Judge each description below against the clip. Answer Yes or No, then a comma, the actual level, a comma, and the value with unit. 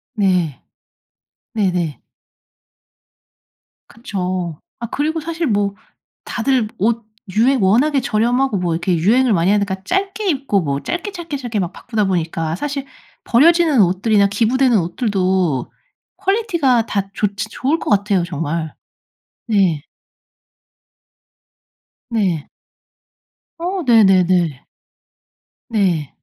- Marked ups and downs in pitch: Yes, wide, 6.4 semitones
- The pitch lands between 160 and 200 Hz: No, high, 210 Hz